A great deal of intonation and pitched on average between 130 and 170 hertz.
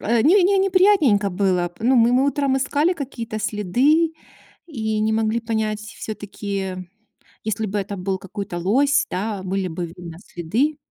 No: wide, 6.2 semitones; high, 220 Hz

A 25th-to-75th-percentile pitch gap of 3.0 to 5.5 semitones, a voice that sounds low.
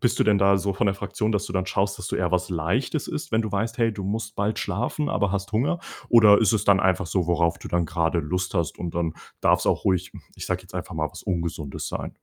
Yes: average, 3.4 semitones; very low, 95 Hz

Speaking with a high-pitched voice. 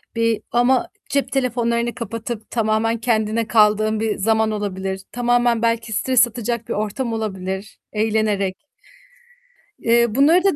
Yes: high, 225 Hz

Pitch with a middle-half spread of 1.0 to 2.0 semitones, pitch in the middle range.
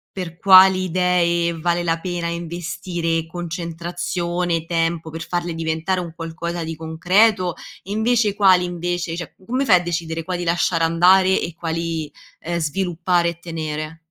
Yes: narrow, 1.6 semitones; medium, 170 Hz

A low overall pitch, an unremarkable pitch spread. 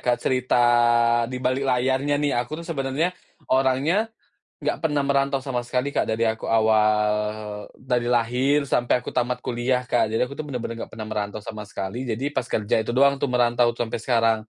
Yes: low, 125 Hz; average, 3.2 semitones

